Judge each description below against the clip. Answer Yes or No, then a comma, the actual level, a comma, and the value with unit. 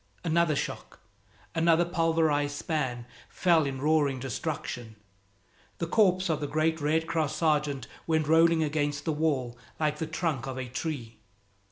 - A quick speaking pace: No, average, 145 wpm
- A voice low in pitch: No, medium, 155 Hz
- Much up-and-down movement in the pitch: No, narrow, 2.6 semitones